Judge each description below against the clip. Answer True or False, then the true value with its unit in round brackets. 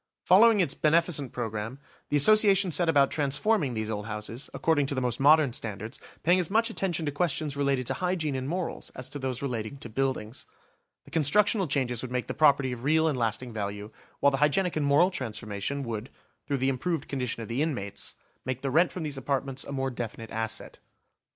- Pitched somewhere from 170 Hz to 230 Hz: False (140 Hz)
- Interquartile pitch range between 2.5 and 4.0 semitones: False (4.8 semitones)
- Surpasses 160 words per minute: True (200 wpm)